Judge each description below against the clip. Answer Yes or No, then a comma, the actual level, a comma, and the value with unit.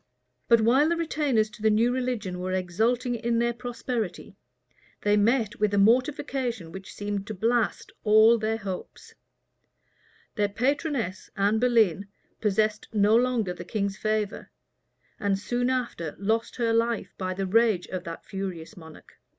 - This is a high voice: Yes, high, 220 Hz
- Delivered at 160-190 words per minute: No, average, 150 wpm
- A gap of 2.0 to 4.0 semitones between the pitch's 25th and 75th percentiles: Yes, average, 3.3 semitones